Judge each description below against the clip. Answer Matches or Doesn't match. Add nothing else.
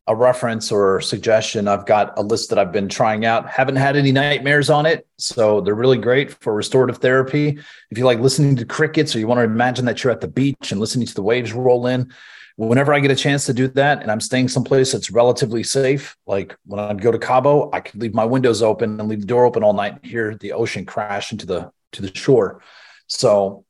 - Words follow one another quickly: Matches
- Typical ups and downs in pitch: Matches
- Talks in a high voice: Doesn't match